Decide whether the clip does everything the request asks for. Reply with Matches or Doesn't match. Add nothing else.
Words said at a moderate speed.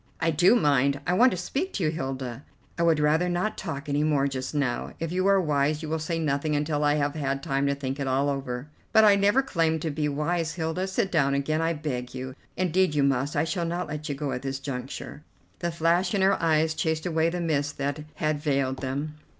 Doesn't match